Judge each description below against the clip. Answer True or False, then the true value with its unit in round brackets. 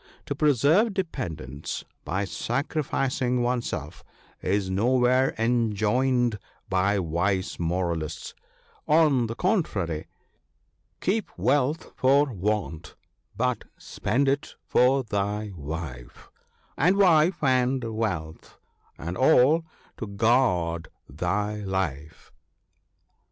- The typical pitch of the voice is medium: False (115 Hz)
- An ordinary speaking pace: False (95 wpm)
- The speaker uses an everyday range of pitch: False (6.5 semitones)